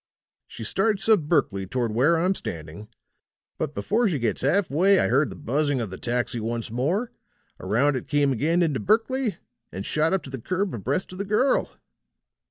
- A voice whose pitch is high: No, medium, 145 Hz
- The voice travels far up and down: Yes, wide, 7.9 semitones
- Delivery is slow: No, average, 185 wpm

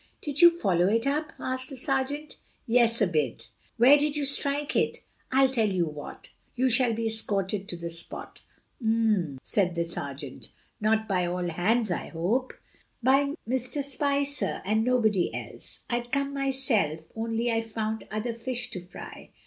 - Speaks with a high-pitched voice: Yes, high, 230 Hz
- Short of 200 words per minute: Yes, average, 165 wpm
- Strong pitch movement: Yes, wide, 5.9 semitones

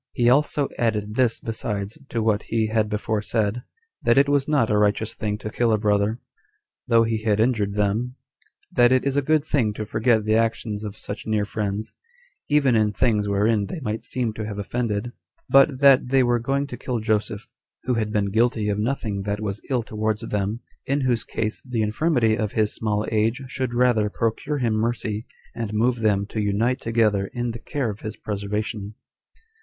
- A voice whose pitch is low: Yes, low, 110 Hz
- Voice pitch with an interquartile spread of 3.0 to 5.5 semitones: No, narrow, 2.6 semitones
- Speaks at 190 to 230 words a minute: Yes, average, 195 wpm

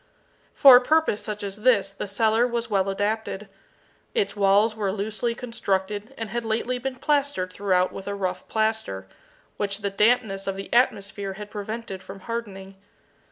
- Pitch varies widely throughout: No, average, 2.9 semitones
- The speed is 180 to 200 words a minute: No, average, 160 wpm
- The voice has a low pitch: No, high, 210 Hz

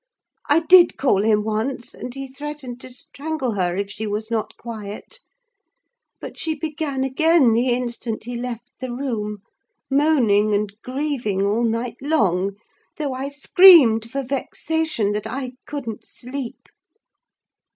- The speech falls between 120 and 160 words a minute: Yes, average, 140 wpm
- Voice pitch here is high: Yes, high, 245 Hz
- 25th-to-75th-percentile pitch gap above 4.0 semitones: Yes, average, 4.5 semitones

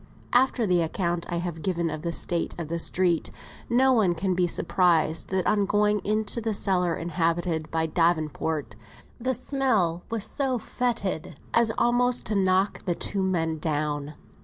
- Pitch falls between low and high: Yes, medium, 180 Hz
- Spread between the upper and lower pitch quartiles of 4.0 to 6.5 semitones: Yes, average, 4.4 semitones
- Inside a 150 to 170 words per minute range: Yes, average, 160 wpm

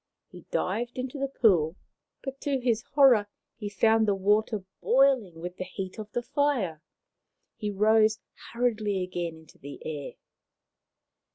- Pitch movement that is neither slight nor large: Yes, average, 4.9 semitones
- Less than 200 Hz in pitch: No, high, 215 Hz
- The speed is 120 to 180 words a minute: Yes, average, 145 wpm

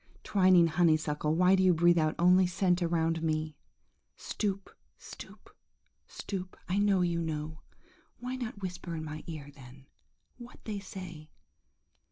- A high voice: No, medium, 175 Hz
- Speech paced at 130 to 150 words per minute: Yes, average, 140 wpm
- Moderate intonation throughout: Yes, average, 3.1 semitones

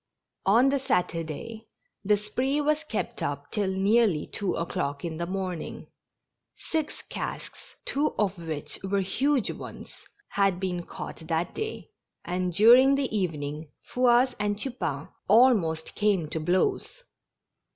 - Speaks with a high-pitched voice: Yes, high, 195 Hz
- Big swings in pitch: Yes, wide, 6.4 semitones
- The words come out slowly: Yes, slow, 130 wpm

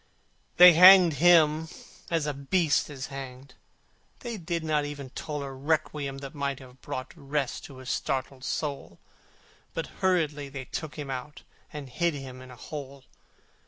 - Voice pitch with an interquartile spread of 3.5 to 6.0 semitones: No, average, 2.8 semitones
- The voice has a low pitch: No, medium, 145 Hz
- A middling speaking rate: Yes, average, 160 wpm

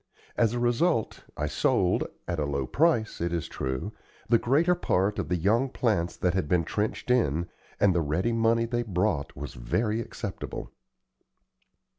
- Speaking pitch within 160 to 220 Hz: No, low, 105 Hz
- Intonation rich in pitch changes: Yes, wide, 5.8 semitones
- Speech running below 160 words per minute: No, average, 165 wpm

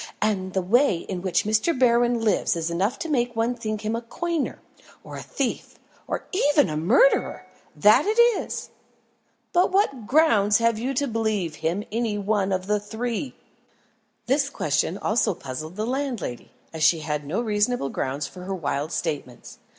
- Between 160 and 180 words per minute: Yes, average, 170 wpm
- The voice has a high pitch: Yes, high, 215 Hz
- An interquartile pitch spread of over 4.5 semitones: Yes, wide, 5.4 semitones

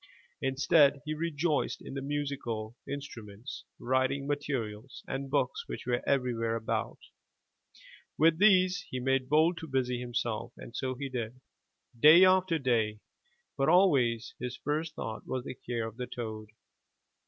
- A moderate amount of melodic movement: Yes, average, 4.0 semitones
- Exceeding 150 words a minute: No, average, 140 wpm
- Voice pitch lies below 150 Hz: Yes, low, 135 Hz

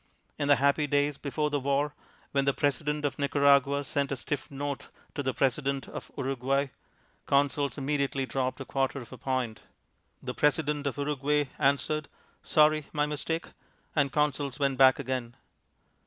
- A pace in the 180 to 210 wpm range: No, average, 155 wpm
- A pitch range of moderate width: No, narrow, 1.4 semitones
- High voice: No, medium, 140 Hz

